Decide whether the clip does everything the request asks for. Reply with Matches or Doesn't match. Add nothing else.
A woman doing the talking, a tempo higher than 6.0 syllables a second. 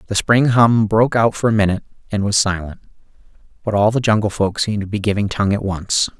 Doesn't match